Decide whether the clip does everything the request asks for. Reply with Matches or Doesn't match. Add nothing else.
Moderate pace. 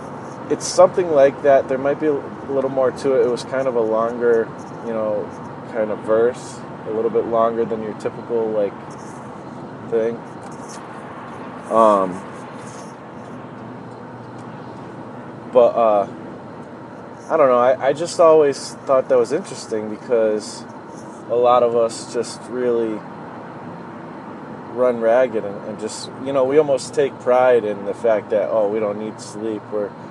Matches